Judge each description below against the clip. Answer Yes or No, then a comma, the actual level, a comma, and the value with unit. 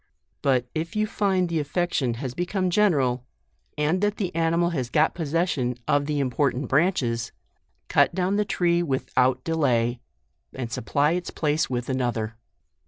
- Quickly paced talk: No, average, 155 wpm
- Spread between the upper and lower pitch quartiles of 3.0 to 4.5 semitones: No, wide, 5.5 semitones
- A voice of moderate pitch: Yes, medium, 150 Hz